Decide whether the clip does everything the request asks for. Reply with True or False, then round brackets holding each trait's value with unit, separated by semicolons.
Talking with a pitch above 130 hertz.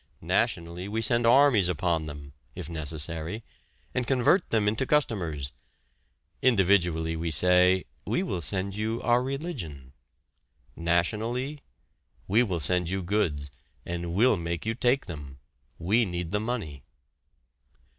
False (90 Hz)